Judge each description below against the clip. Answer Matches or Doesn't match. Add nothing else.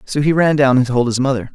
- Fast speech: Matches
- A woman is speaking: Doesn't match